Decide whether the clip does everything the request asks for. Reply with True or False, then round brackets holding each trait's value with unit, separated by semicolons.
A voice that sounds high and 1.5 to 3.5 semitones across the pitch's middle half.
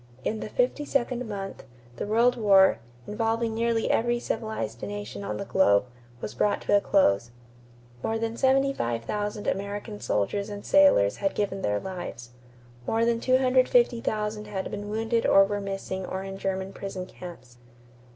True (205 Hz; 3.1 semitones)